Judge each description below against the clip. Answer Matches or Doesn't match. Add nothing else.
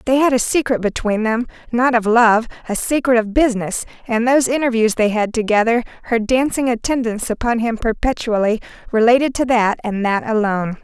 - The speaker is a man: Doesn't match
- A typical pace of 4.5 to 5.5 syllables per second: Doesn't match